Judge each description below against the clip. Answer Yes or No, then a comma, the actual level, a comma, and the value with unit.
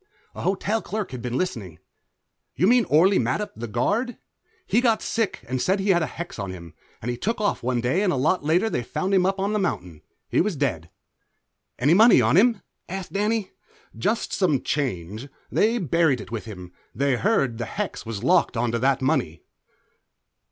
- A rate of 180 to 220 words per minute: Yes, average, 190 wpm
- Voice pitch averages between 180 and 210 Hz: No, medium, 160 Hz